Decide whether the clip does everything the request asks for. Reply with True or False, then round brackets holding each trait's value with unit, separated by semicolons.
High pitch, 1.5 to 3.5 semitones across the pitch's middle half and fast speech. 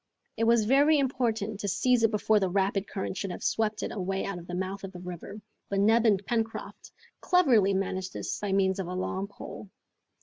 True (200 Hz; 2.8 semitones; 210 wpm)